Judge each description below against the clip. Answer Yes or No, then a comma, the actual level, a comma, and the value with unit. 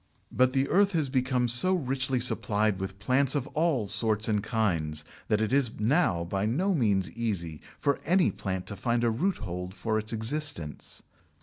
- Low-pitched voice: Yes, low, 115 Hz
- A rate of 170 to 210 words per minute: Yes, average, 175 wpm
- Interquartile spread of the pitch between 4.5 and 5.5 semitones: Yes, average, 5.1 semitones